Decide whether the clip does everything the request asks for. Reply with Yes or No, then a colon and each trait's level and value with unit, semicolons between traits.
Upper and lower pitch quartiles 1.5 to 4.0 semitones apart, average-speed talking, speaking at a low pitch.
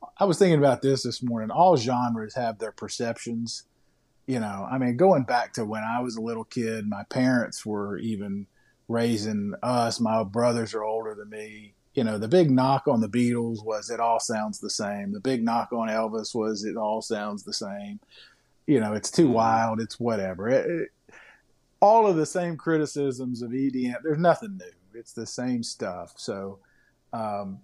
Yes: average, 2.9 semitones; average, 190 wpm; low, 115 Hz